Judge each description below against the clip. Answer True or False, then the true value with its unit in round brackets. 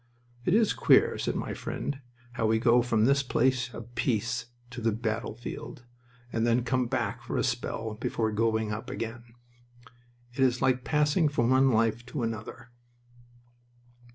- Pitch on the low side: True (120 Hz)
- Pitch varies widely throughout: False (2.4 semitones)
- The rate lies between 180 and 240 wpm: False (155 wpm)